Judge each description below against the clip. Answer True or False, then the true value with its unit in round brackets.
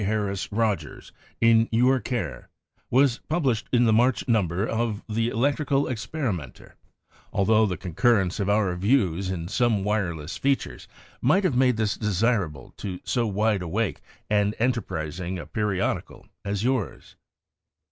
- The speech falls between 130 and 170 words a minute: True (140 wpm)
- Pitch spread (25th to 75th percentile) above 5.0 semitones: False (4.0 semitones)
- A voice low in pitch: True (110 Hz)